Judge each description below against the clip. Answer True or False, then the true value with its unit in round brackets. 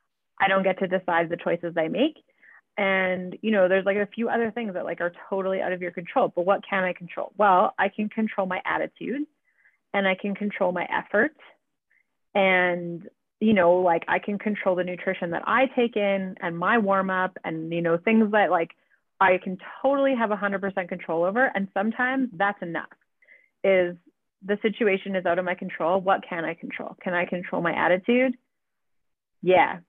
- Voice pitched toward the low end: False (190 Hz)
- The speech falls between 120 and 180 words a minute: False (190 wpm)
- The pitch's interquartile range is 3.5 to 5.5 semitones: False (2.9 semitones)